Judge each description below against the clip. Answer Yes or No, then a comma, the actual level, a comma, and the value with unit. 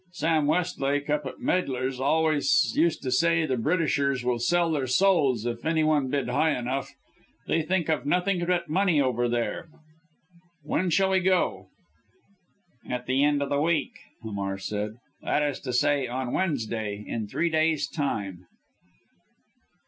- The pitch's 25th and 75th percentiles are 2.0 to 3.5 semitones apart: No, average, 4.8 semitones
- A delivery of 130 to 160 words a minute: Yes, average, 155 wpm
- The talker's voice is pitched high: No, medium, 145 Hz